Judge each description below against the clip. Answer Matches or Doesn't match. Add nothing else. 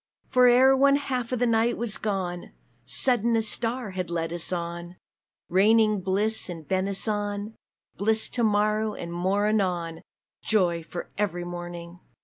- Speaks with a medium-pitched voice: Doesn't match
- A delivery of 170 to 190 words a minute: Doesn't match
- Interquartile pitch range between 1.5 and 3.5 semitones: Doesn't match